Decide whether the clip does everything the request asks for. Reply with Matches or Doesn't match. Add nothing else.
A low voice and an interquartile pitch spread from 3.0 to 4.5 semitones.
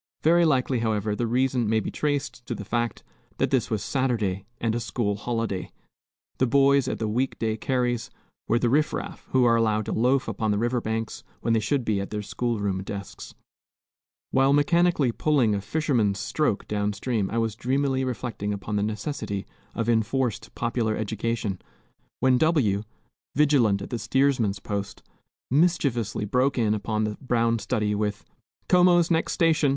Matches